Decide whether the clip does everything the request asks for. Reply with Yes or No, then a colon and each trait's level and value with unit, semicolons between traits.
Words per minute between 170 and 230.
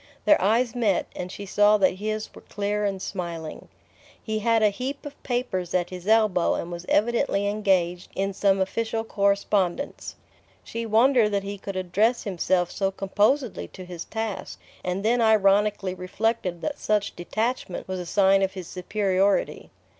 No: average, 160 wpm